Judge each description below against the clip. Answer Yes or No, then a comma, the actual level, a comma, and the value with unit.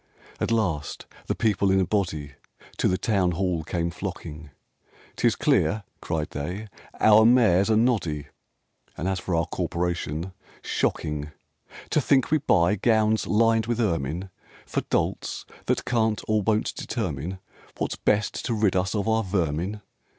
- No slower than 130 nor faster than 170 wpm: Yes, average, 150 wpm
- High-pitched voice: No, very low, 95 Hz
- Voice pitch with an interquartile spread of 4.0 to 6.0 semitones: Yes, average, 4.5 semitones